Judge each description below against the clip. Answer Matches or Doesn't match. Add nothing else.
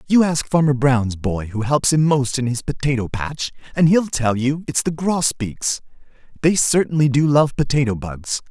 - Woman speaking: Doesn't match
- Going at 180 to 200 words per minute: Matches